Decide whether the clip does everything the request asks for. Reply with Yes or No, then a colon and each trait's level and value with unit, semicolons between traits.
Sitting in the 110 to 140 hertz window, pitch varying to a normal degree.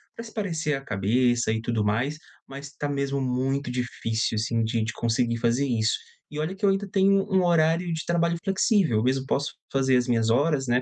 No: low, 135 Hz; wide, 6.0 semitones